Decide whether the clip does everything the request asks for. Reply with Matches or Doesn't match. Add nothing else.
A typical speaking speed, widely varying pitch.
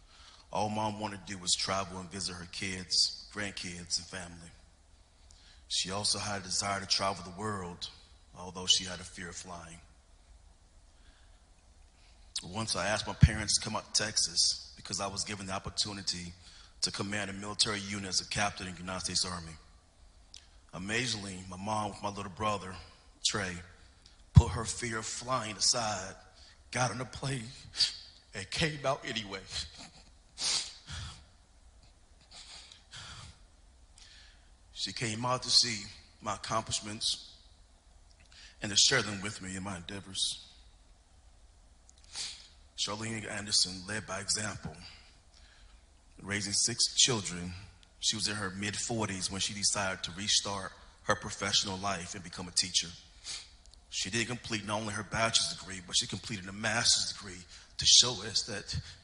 Doesn't match